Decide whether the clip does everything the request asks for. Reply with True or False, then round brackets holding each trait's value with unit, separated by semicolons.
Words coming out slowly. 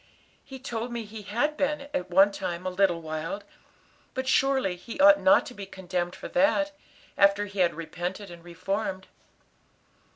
False (165 wpm)